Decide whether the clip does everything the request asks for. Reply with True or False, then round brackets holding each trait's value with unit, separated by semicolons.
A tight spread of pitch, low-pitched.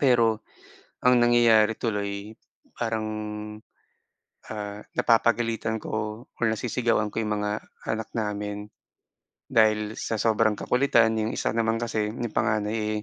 True (1.4 semitones; 110 Hz)